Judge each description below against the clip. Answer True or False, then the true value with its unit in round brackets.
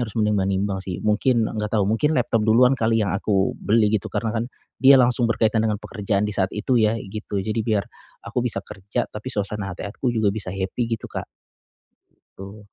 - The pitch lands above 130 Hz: False (105 Hz)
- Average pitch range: False (2.3 semitones)